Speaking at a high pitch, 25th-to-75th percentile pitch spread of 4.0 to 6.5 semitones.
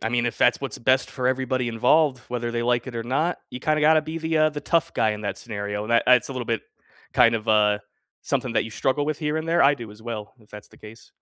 No: low, 120 Hz; average, 4.5 semitones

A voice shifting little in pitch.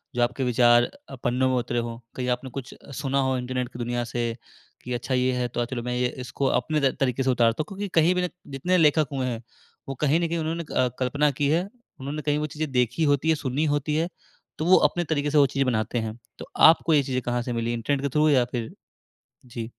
No: average, 3.6 semitones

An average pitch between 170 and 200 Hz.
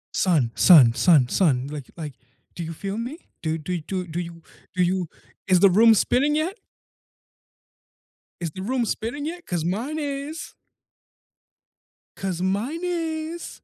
Yes: high, 190 Hz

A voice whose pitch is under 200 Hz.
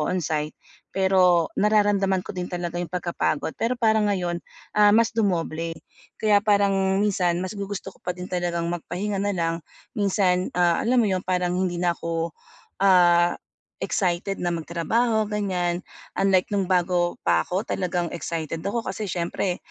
Yes: medium, 185 Hz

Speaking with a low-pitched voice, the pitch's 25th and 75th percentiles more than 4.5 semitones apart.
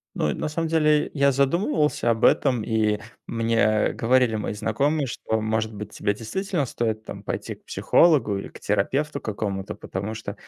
Yes: low, 115 Hz; average, 5.2 semitones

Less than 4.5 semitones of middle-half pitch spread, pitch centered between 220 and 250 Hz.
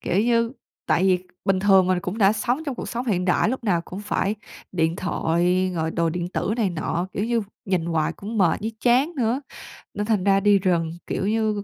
No: average, 3.8 semitones; high, 195 Hz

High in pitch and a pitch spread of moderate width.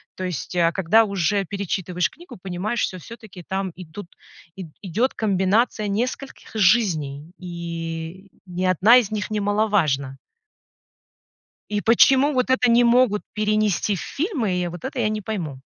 Yes: high, 200 Hz; average, 3.9 semitones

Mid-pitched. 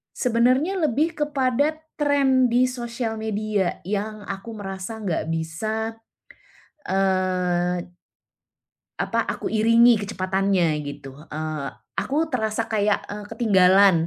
No: high, 215 Hz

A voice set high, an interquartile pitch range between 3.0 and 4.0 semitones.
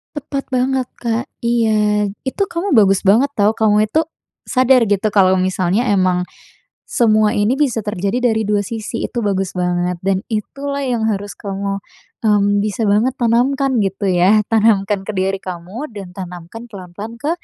Yes: high, 210 Hz; average, 3.5 semitones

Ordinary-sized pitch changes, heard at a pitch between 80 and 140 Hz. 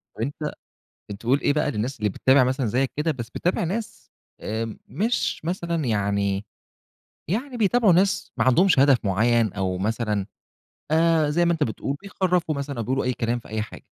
No: wide, 7.1 semitones; low, 135 Hz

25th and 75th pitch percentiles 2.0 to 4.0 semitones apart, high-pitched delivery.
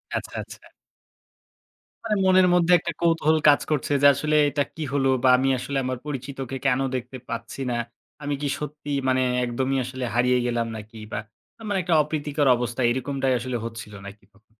No: average, 3.3 semitones; low, 135 Hz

